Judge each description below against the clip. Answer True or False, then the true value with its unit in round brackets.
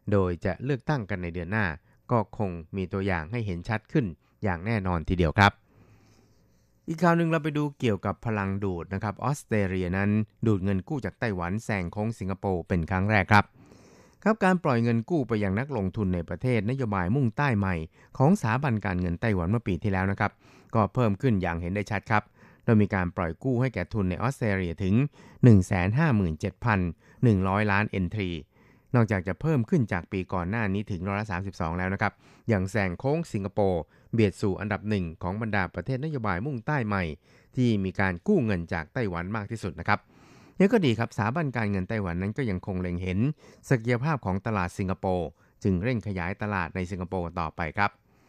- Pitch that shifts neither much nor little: True (3.9 semitones)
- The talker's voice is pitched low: True (100 Hz)